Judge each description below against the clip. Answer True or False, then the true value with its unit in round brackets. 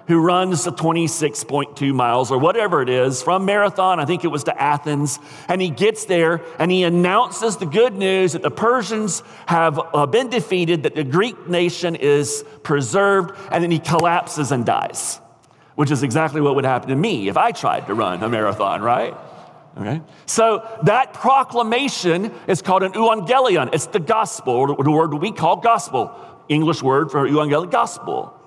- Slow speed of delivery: False (175 wpm)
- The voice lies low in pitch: False (170 Hz)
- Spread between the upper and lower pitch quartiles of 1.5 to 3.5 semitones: False (4.6 semitones)